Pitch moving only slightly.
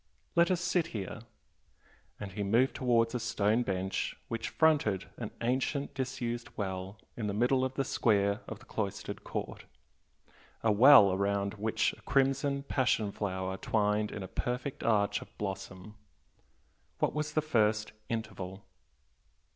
No: average, 4.4 semitones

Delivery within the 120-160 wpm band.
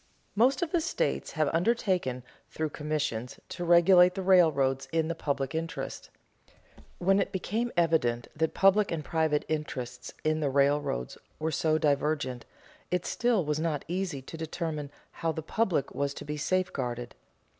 Yes: average, 155 wpm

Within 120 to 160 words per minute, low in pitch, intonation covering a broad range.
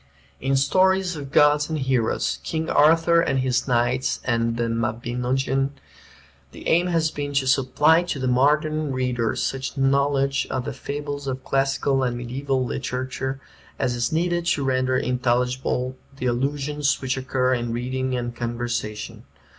No: average, 145 wpm; low, 130 Hz; narrow, 2.5 semitones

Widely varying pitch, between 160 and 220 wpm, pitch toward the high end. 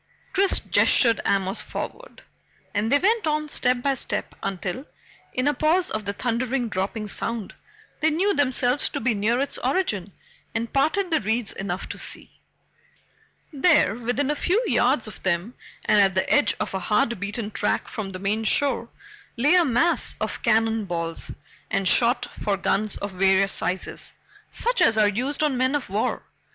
Yes: wide, 6.0 semitones; average, 170 wpm; high, 235 Hz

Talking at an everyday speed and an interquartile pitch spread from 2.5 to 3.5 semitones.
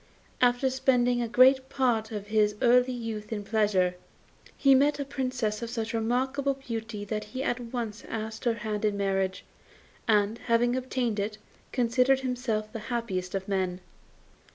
Yes: average, 155 wpm; average, 3.0 semitones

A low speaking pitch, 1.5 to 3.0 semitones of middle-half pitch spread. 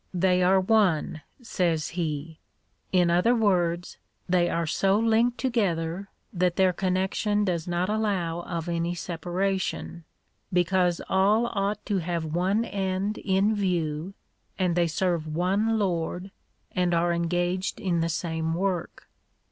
No: medium, 180 Hz; narrow, 2.5 semitones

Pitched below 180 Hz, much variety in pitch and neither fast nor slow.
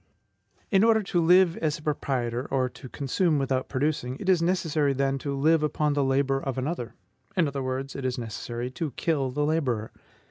No: medium, 140 Hz; average, 3.7 semitones; average, 190 wpm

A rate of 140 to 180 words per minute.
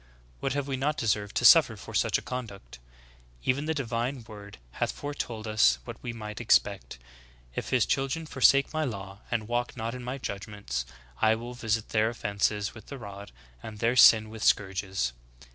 No: average, 190 wpm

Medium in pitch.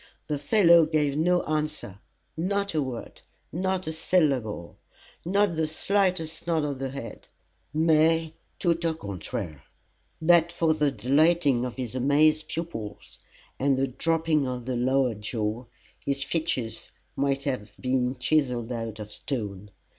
Yes: medium, 145 Hz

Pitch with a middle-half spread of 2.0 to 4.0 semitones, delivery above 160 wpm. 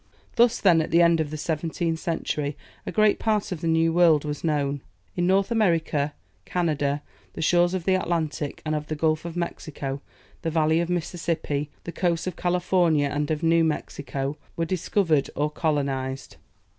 Yes: average, 2.8 semitones; average, 180 wpm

